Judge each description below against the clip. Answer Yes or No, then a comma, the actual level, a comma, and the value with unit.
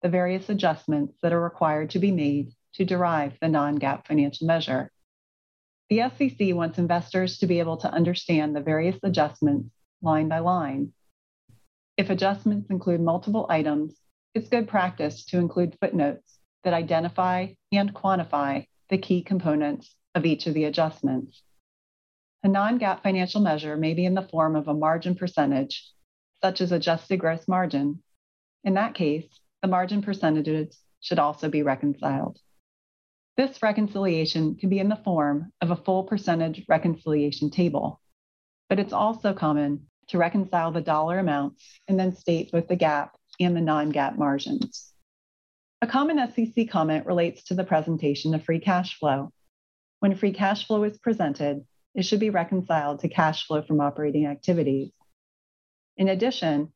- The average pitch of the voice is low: No, medium, 165 Hz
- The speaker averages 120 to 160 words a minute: Yes, average, 150 wpm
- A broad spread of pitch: No, average, 4.2 semitones